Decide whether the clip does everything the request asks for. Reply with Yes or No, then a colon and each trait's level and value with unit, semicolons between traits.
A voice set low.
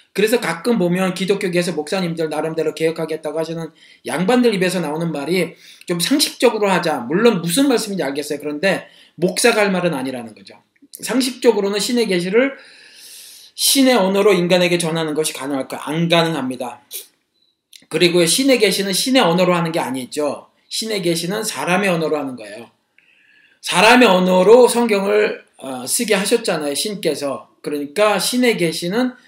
No: medium, 185 Hz